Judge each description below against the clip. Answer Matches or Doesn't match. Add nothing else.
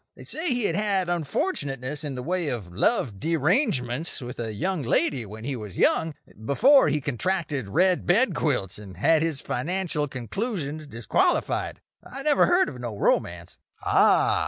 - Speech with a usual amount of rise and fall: Doesn't match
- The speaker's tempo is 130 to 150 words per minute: Doesn't match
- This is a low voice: Doesn't match